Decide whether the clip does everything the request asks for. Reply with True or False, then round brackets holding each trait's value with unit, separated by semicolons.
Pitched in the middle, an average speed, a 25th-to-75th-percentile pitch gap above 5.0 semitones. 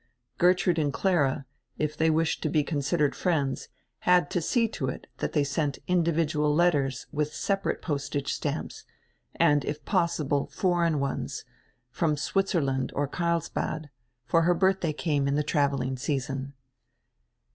False (150 Hz; 145 wpm; 3.3 semitones)